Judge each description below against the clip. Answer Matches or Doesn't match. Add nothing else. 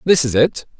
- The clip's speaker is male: Matches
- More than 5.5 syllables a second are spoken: Doesn't match